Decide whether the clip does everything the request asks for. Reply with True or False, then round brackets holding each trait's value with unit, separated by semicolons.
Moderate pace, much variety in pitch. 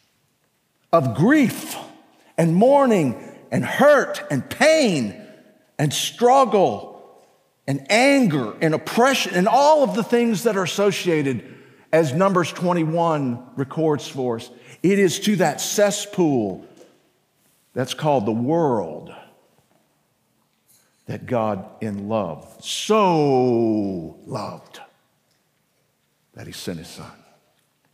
False (105 wpm; 8.4 semitones)